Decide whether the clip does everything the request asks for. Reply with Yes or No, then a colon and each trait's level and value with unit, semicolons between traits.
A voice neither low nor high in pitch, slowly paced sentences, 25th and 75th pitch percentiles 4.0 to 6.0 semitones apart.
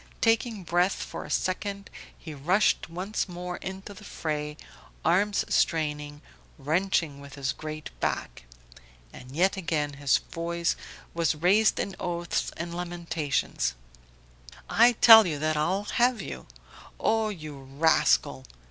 Yes: medium, 170 Hz; slow, 130 wpm; average, 4.5 semitones